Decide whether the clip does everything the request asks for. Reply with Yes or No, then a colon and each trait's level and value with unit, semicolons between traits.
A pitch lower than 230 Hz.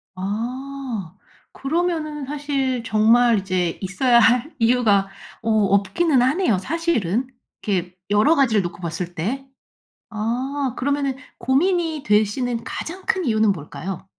No: high, 235 Hz